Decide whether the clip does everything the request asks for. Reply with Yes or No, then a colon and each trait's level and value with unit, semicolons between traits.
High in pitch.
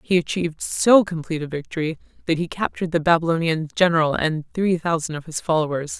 No: medium, 165 Hz